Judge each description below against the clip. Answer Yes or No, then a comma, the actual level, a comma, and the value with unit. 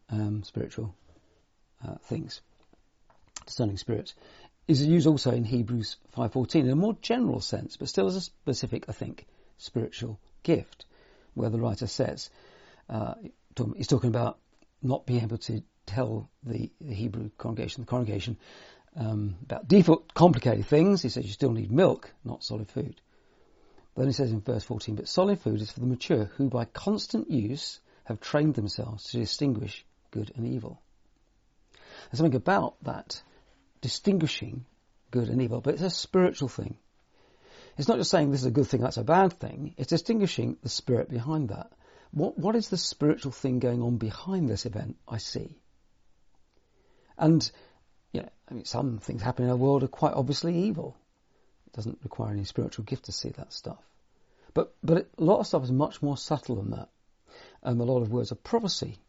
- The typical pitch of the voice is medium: No, low, 125 Hz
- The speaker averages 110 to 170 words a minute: No, average, 180 wpm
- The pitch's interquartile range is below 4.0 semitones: No, average, 5.2 semitones